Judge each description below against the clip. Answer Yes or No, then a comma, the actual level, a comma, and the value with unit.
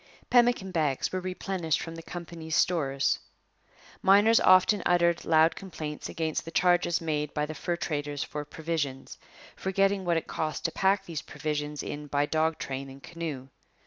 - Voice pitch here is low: No, medium, 165 Hz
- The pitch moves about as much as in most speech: Yes, average, 3.3 semitones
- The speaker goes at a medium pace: Yes, average, 160 wpm